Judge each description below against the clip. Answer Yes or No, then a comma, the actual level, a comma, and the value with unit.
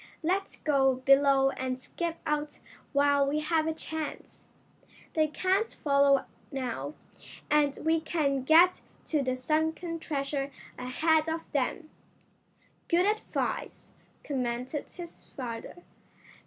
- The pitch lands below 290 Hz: No, very high, 295 Hz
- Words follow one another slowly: Yes, slow, 115 wpm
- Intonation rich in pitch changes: No, average, 2.9 semitones